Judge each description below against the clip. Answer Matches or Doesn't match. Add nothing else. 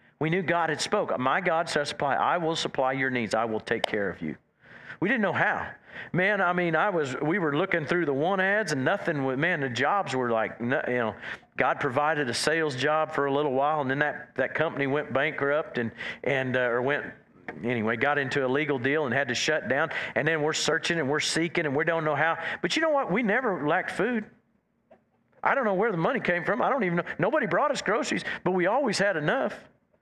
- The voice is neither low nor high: Matches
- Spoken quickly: Matches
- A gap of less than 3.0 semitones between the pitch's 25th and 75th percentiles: Doesn't match